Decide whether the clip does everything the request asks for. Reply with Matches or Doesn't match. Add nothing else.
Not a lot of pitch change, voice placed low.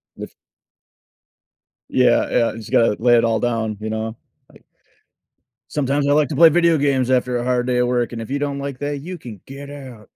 Doesn't match